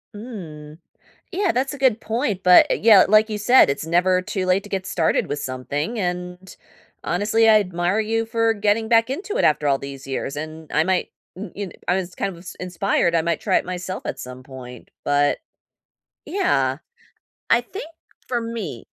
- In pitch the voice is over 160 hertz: Yes, medium, 185 Hz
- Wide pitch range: Yes, wide, 5.9 semitones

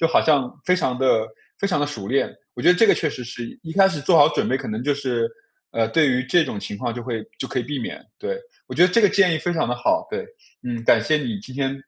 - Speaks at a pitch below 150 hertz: Yes, low, 135 Hz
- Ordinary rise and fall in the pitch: No, wide, 5.7 semitones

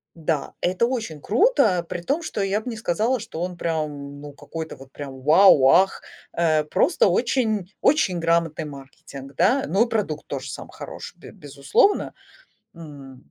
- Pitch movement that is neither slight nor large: No, wide, 6.6 semitones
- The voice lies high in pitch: No, medium, 170 Hz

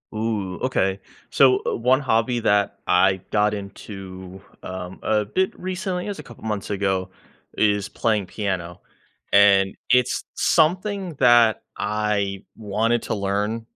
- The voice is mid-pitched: No, low, 105 Hz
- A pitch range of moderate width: Yes, average, 3.6 semitones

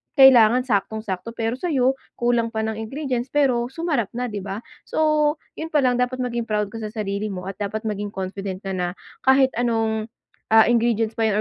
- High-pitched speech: Yes, high, 225 Hz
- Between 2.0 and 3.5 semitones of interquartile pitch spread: Yes, average, 3.2 semitones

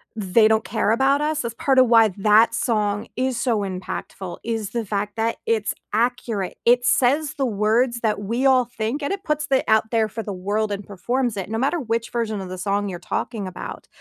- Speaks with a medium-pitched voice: No, high, 225 Hz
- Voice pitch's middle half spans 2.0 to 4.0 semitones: Yes, average, 3.2 semitones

